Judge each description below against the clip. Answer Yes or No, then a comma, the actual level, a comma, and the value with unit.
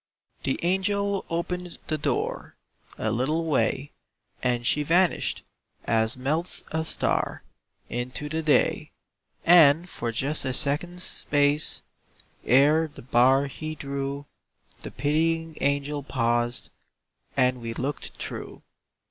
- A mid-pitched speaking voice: Yes, medium, 145 Hz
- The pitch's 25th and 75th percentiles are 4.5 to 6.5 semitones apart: No, average, 4.0 semitones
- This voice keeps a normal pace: No, slow, 115 wpm